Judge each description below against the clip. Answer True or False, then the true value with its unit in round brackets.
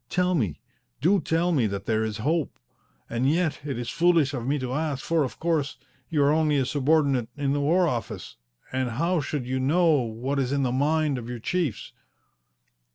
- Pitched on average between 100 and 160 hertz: True (140 Hz)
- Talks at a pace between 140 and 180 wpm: False (200 wpm)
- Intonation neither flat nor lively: True (4.2 semitones)